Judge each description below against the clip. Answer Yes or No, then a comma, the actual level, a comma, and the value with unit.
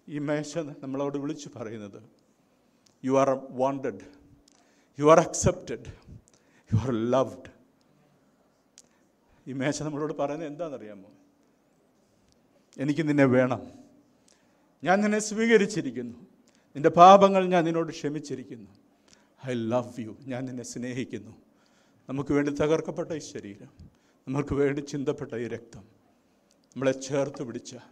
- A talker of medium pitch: Yes, medium, 145 Hz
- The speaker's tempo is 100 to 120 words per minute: Yes, average, 105 wpm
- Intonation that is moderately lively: Yes, average, 4.4 semitones